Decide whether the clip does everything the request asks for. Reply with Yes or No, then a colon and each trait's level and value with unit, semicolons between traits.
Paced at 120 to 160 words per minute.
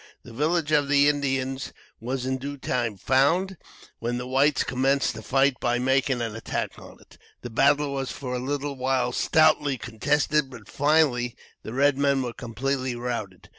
No: average, 170 wpm